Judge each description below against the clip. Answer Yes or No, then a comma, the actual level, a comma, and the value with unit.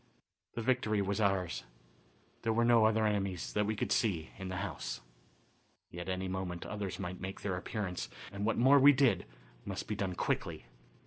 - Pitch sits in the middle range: No, low, 100 Hz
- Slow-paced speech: No, average, 185 wpm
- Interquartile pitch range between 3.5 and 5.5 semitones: No, average, 3.0 semitones